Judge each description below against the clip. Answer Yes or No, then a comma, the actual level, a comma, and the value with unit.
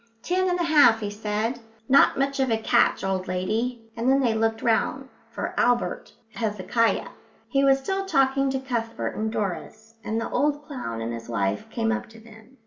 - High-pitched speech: Yes, high, 230 Hz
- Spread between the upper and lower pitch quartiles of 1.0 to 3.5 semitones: No, average, 3.9 semitones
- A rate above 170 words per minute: Yes, average, 190 wpm